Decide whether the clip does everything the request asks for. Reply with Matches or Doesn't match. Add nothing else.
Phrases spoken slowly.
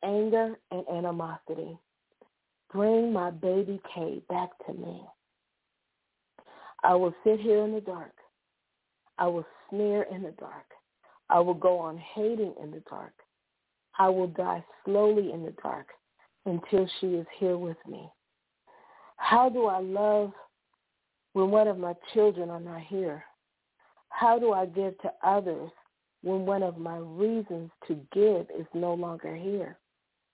Doesn't match